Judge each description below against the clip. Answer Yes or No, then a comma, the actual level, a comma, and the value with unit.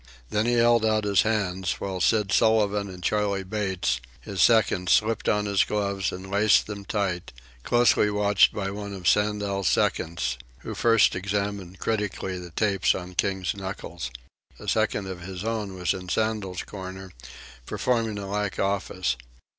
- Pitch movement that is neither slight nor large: No, narrow, 2.1 semitones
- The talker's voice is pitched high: No, low, 100 Hz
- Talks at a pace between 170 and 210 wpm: No, average, 155 wpm